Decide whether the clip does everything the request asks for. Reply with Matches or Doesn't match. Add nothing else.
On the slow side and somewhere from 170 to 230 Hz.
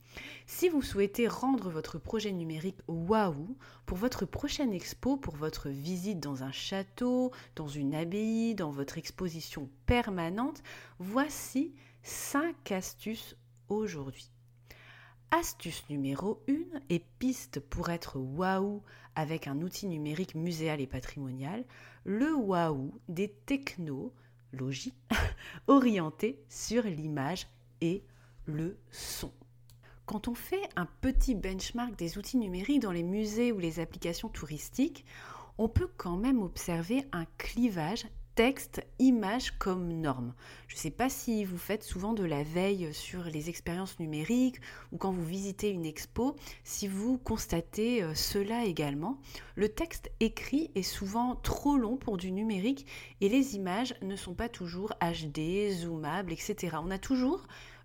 Matches